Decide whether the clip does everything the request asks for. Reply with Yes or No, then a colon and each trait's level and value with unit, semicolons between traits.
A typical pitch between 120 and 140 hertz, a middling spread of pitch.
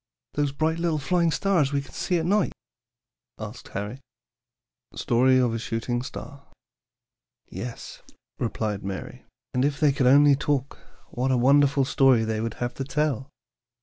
Yes: low, 135 Hz; average, 3.4 semitones